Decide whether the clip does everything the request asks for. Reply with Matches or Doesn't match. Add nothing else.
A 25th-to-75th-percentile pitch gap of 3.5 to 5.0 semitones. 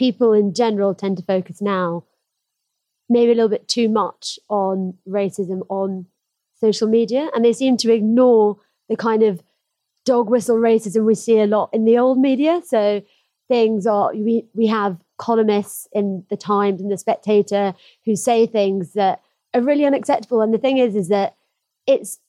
Doesn't match